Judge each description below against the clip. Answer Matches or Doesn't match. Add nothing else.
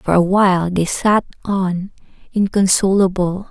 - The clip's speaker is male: Doesn't match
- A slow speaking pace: Matches